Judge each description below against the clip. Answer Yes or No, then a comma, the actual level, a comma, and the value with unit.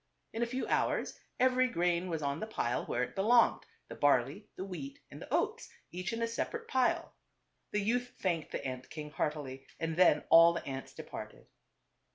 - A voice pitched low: No, medium, 180 Hz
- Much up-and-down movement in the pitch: Yes, wide, 7.7 semitones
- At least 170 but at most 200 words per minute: Yes, average, 190 wpm